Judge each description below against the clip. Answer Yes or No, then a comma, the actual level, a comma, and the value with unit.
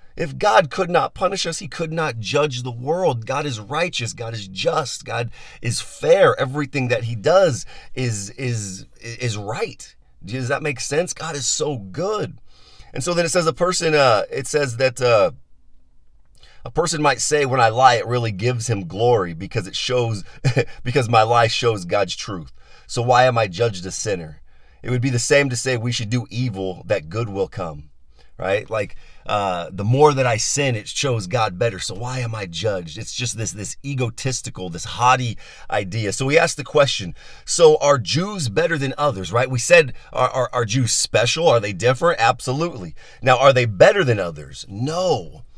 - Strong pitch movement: No, average, 4.1 semitones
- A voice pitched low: Yes, low, 125 Hz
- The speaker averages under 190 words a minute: No, average, 195 wpm